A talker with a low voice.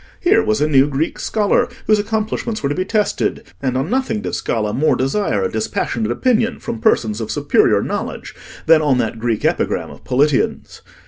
No: medium, 150 Hz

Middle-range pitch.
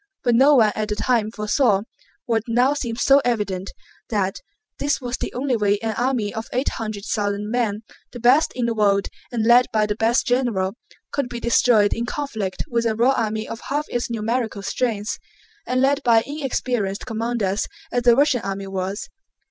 No: high, 230 Hz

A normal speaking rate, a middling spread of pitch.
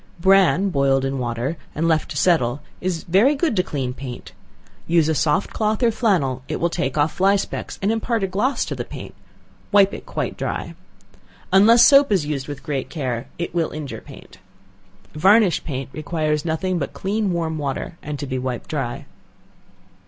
No: average, 180 wpm; wide, 6.0 semitones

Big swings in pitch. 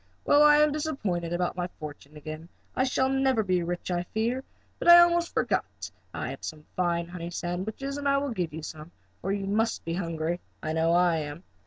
Yes: wide, 7.9 semitones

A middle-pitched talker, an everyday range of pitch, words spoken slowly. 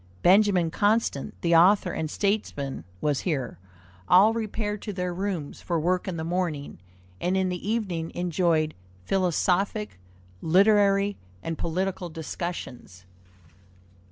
Yes: medium, 180 Hz; average, 3.4 semitones; slow, 120 wpm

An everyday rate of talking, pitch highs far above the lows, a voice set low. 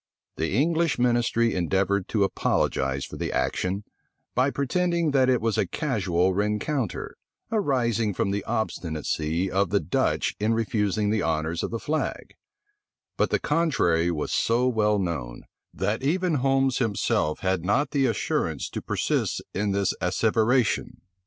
Yes: average, 145 wpm; wide, 5.9 semitones; low, 105 Hz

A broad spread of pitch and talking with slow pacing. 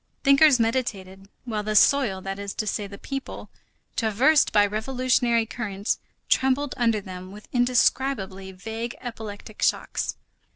No: average, 4.1 semitones; slow, 130 wpm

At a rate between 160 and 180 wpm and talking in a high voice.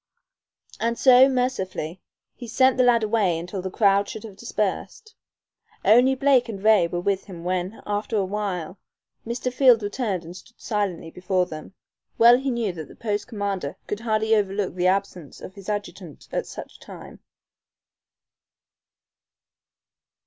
No: average, 150 wpm; high, 205 Hz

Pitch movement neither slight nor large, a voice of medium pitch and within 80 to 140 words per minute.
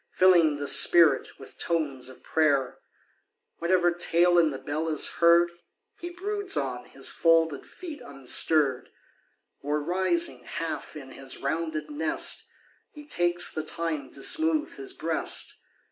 Yes: average, 3.4 semitones; medium, 165 Hz; slow, 135 wpm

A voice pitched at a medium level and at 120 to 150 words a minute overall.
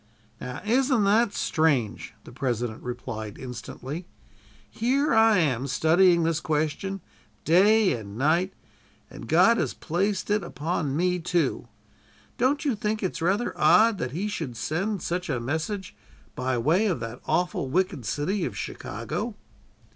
Yes: medium, 170 Hz; average, 140 wpm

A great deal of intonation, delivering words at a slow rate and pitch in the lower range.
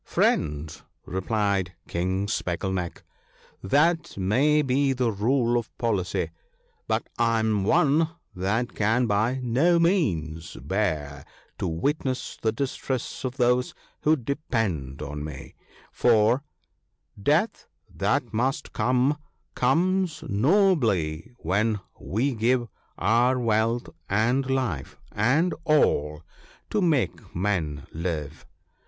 Yes: wide, 6.4 semitones; slow, 115 wpm; low, 115 Hz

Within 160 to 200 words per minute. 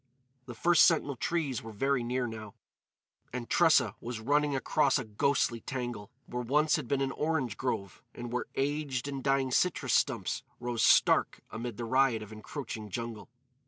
Yes: average, 165 wpm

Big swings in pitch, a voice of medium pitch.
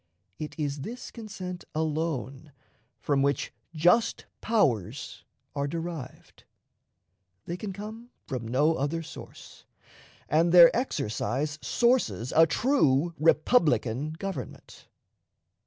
No: average, 4.8 semitones; medium, 160 Hz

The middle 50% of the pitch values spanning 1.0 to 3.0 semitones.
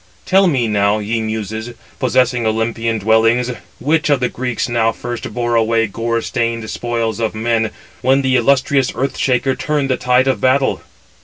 Yes: narrow, 2.4 semitones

